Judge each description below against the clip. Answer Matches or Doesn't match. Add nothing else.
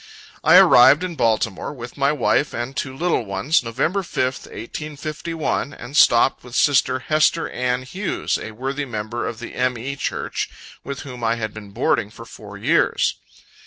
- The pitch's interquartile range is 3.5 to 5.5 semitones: Matches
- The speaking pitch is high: Doesn't match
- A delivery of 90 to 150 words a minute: Doesn't match